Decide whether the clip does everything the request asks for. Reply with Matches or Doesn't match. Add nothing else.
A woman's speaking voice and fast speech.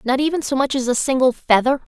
Matches